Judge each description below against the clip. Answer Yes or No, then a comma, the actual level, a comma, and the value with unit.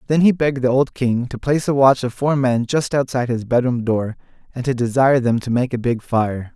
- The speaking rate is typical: No, fast, 245 wpm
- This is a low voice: Yes, low, 125 Hz